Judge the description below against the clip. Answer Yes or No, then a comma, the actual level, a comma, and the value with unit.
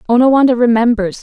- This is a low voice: No, high, 240 Hz